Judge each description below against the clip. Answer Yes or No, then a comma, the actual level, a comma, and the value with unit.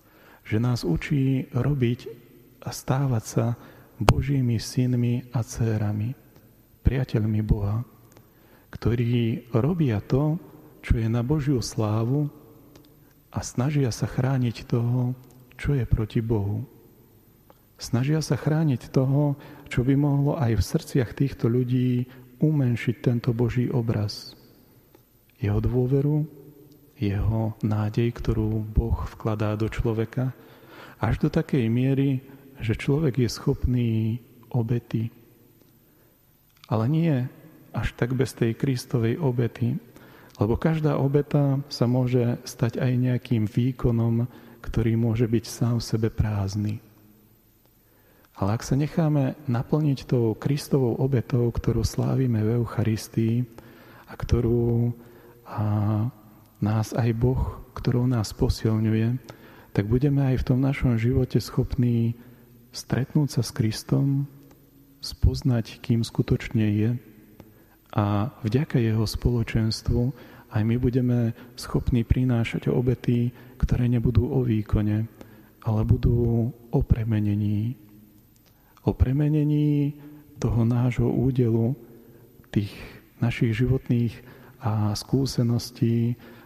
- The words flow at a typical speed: No, slow, 105 wpm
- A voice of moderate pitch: No, low, 120 Hz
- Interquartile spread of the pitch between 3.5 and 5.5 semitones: No, average, 2.7 semitones